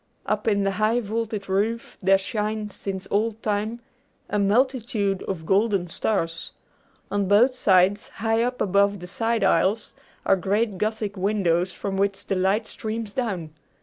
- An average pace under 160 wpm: Yes, average, 150 wpm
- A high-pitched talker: Yes, high, 205 Hz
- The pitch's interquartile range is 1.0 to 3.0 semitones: Yes, narrow, 2.4 semitones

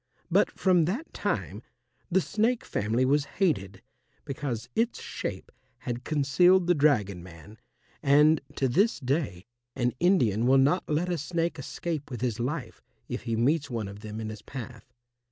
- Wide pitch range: Yes, wide, 6.7 semitones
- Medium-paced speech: Yes, average, 160 wpm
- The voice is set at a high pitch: No, low, 135 Hz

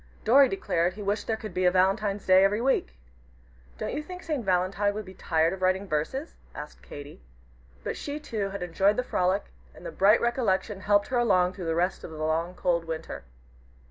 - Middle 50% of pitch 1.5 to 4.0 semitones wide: Yes, average, 3.6 semitones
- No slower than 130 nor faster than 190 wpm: No, fast, 205 wpm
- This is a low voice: No, high, 195 Hz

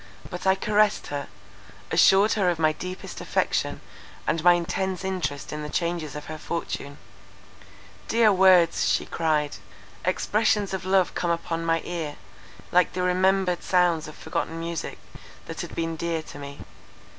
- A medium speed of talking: Yes, average, 150 wpm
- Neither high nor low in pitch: Yes, medium, 170 Hz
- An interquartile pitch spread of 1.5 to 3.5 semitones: Yes, average, 2.9 semitones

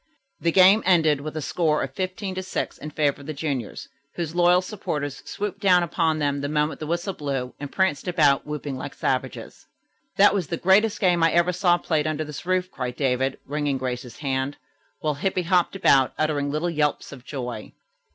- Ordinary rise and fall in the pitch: Yes, average, 4.1 semitones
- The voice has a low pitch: No, medium, 155 Hz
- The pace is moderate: Yes, average, 190 wpm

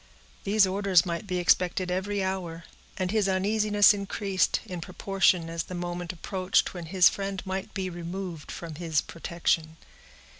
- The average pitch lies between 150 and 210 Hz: Yes, medium, 185 Hz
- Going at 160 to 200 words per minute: No, average, 150 wpm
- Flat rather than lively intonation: Yes, narrow, 2.3 semitones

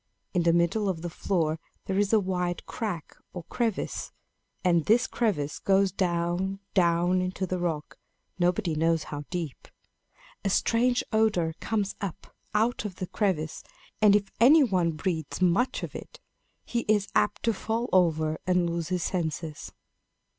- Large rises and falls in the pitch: No, average, 3.6 semitones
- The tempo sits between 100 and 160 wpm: Yes, average, 155 wpm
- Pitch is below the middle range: No, medium, 185 Hz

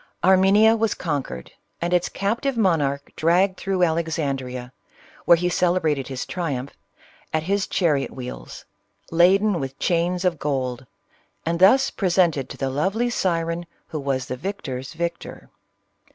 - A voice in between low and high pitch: Yes, medium, 170 Hz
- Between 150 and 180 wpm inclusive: No, average, 140 wpm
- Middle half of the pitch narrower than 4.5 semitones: No, average, 5.3 semitones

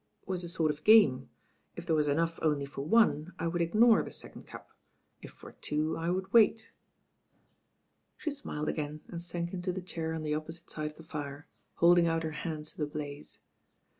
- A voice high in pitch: No, medium, 165 Hz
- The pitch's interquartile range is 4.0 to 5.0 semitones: No, average, 2.7 semitones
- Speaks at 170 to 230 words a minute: Yes, average, 200 wpm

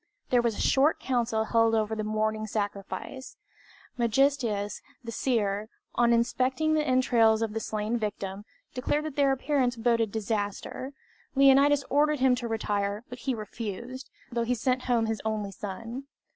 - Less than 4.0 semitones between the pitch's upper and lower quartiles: Yes, average, 3.3 semitones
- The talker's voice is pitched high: Yes, high, 230 Hz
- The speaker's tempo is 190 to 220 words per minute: No, average, 155 wpm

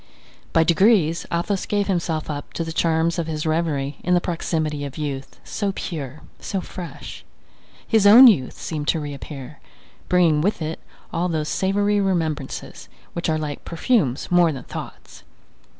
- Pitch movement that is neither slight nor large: Yes, average, 3.1 semitones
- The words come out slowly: No, average, 155 wpm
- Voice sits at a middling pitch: Yes, medium, 165 Hz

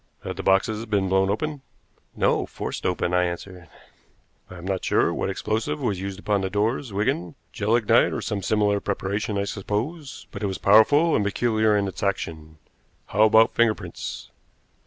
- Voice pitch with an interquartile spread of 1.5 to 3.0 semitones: Yes, narrow, 2.4 semitones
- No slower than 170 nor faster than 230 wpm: Yes, average, 175 wpm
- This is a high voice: No, low, 100 Hz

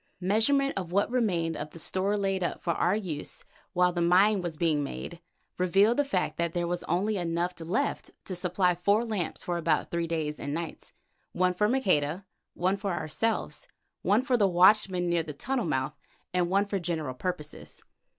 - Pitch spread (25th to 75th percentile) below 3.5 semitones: Yes, average, 3.1 semitones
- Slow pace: No, average, 185 wpm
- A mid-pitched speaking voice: Yes, medium, 180 Hz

